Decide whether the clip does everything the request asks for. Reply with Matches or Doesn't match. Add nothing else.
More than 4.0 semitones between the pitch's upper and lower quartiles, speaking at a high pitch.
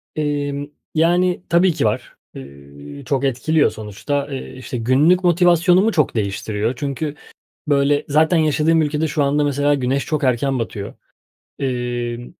Doesn't match